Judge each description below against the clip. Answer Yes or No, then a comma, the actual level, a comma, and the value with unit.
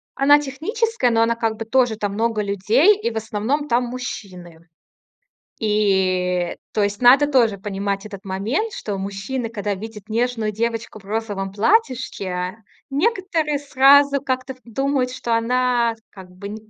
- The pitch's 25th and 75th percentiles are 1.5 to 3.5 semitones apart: No, average, 4.6 semitones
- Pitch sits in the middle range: No, high, 225 Hz